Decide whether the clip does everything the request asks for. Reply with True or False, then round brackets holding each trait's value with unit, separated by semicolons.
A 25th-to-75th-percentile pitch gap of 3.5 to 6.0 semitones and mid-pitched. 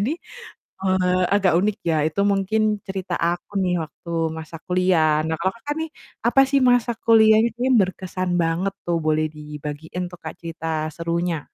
True (4.0 semitones; 180 Hz)